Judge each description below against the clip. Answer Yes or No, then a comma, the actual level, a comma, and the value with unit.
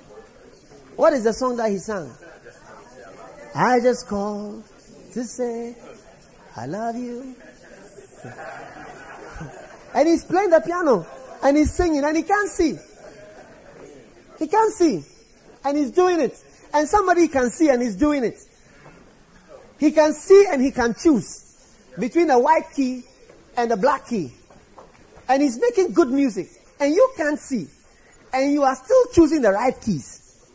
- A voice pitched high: Yes, very high, 270 Hz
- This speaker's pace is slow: No, average, 145 wpm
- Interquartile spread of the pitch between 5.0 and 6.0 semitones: Yes, wide, 5.5 semitones